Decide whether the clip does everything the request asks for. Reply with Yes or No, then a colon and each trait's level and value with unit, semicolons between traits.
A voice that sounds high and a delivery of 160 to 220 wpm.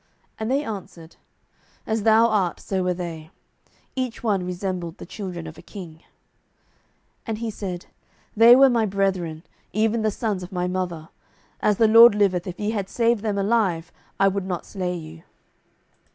Yes: high, 195 Hz; average, 170 wpm